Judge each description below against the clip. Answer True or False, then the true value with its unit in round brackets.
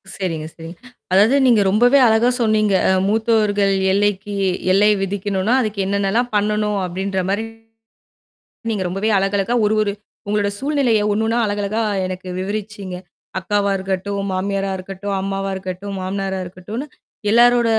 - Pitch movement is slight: True (1.9 semitones)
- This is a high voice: True (200 Hz)